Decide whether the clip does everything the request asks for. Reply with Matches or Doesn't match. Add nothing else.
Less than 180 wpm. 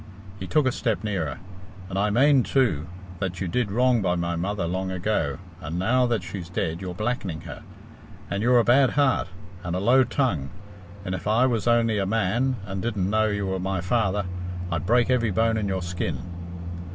Doesn't match